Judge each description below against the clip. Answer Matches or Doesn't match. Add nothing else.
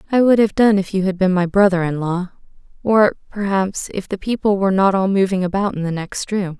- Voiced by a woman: Matches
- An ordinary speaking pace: Doesn't match